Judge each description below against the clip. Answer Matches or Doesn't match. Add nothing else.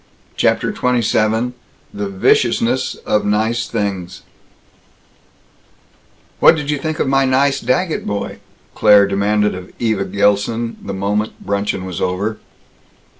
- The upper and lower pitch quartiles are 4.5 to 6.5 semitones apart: Doesn't match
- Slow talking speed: Matches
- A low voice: Matches